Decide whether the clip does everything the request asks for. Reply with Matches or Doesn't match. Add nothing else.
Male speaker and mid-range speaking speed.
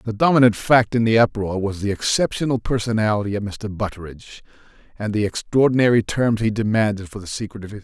Matches